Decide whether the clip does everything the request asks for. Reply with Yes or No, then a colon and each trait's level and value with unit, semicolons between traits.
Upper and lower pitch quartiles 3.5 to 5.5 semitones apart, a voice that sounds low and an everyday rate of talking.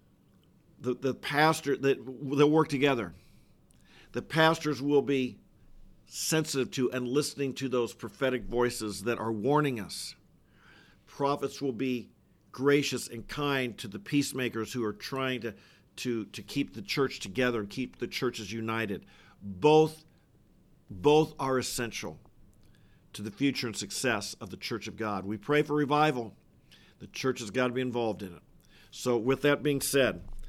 Yes: average, 4.0 semitones; low, 130 Hz; average, 155 wpm